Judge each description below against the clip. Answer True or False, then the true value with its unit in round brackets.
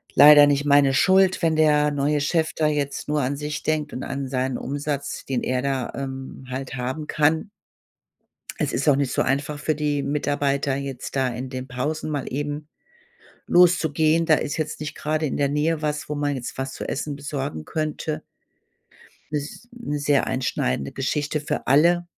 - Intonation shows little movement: True (2.1 semitones)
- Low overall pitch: False (145 Hz)